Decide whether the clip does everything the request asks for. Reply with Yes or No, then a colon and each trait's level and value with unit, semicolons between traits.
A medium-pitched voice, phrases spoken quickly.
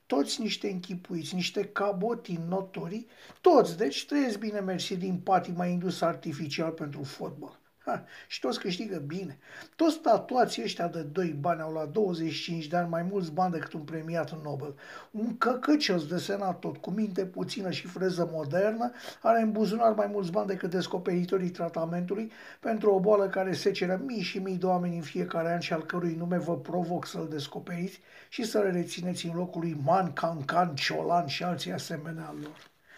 Yes: medium, 180 Hz; fast, 180 wpm